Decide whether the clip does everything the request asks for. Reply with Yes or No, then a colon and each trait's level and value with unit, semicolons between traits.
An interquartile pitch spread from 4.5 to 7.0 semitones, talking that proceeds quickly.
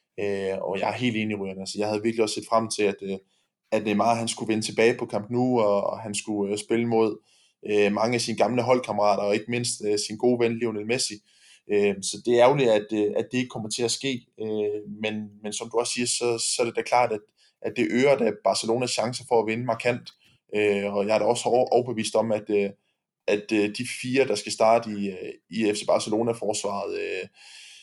No: narrow, 2.4 semitones; fast, 235 wpm